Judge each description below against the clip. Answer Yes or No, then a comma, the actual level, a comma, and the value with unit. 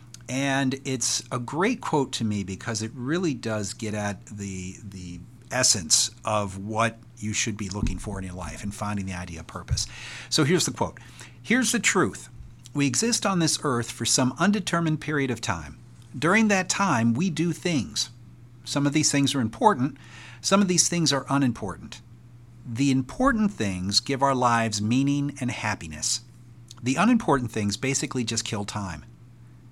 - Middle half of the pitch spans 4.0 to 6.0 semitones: Yes, average, 4.5 semitones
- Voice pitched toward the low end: Yes, low, 120 Hz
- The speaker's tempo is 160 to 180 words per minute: Yes, average, 170 wpm